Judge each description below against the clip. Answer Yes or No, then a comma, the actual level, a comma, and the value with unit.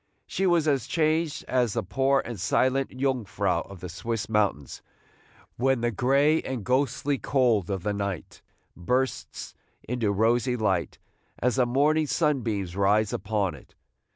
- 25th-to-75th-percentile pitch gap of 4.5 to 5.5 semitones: Yes, average, 4.9 semitones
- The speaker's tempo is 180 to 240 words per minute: No, average, 145 wpm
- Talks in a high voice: No, low, 120 Hz